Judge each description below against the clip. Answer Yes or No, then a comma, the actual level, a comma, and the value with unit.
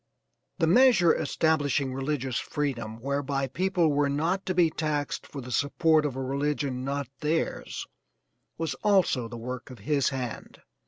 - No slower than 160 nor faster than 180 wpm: No, average, 150 wpm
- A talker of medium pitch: Yes, medium, 145 Hz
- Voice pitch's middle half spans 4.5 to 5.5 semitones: No, average, 3.3 semitones